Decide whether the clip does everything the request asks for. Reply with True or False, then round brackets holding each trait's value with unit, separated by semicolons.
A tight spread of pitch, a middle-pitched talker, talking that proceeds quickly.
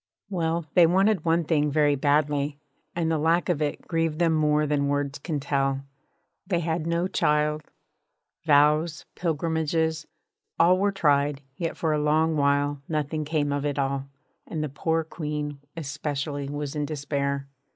False (2.2 semitones; 150 Hz; 160 wpm)